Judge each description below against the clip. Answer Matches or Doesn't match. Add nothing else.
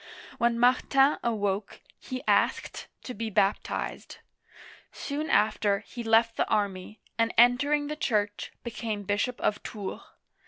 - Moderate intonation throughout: Matches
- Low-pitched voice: Doesn't match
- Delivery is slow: Matches